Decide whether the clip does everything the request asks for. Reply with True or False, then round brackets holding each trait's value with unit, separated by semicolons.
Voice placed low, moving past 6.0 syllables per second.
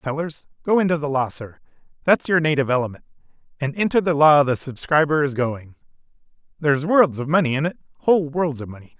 False (150 Hz; 6.2 syllables/s)